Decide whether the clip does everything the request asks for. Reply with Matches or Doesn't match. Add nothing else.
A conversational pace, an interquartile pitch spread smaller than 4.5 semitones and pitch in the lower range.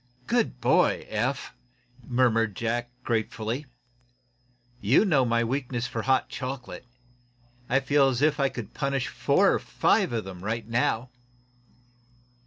Doesn't match